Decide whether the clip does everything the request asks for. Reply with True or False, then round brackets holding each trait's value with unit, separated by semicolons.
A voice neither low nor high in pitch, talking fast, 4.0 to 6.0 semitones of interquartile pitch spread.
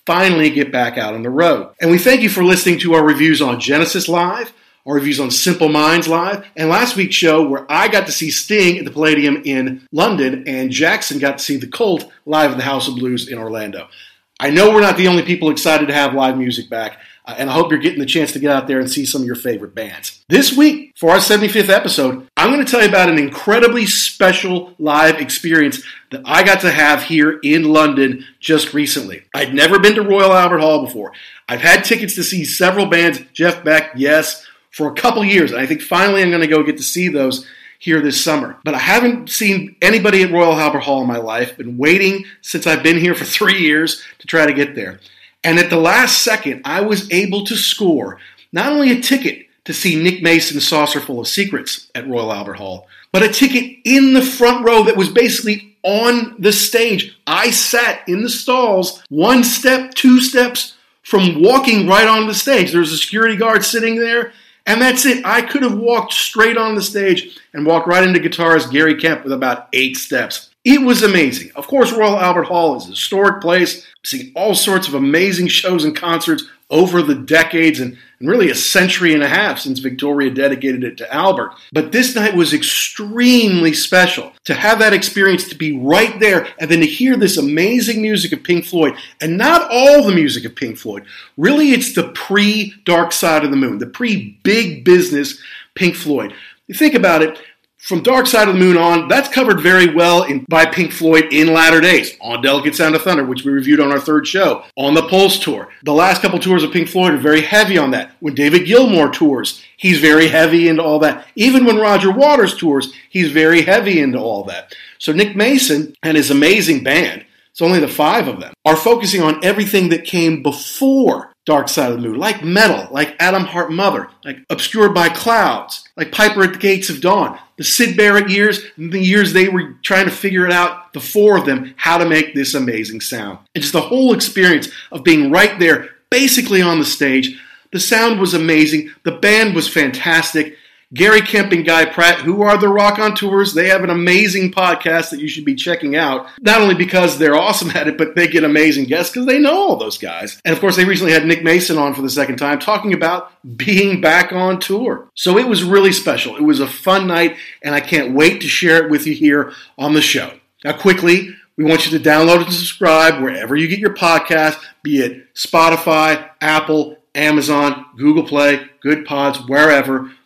True (175 Hz; 215 wpm; 5.3 semitones)